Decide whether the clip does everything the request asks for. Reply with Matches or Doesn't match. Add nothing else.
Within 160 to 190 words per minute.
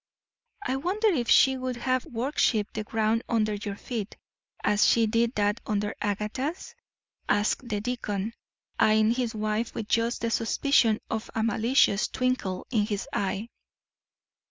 Doesn't match